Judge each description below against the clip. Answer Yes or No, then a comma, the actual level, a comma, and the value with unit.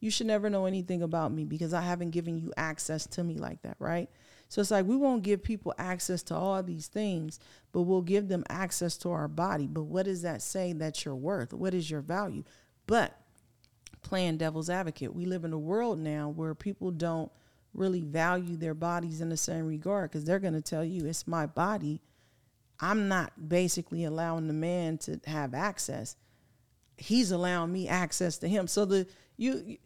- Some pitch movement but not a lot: Yes, average, 3.2 semitones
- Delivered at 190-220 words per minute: Yes, average, 195 wpm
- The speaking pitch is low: No, medium, 170 Hz